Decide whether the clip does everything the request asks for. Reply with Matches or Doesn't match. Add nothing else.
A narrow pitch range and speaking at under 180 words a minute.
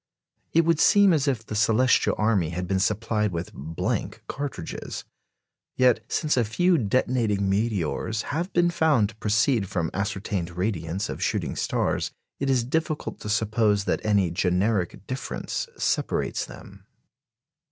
Doesn't match